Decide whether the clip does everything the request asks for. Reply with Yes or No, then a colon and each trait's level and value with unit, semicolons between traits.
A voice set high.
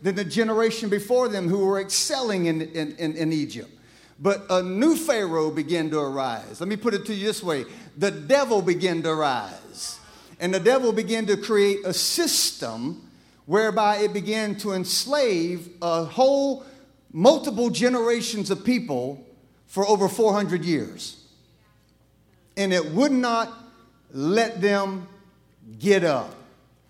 Yes: high, 200 Hz